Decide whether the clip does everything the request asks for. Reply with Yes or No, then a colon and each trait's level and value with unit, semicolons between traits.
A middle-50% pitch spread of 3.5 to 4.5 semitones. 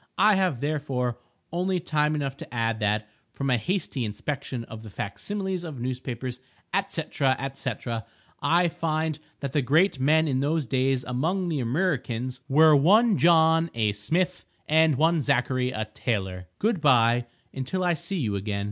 No: average, 5.0 semitones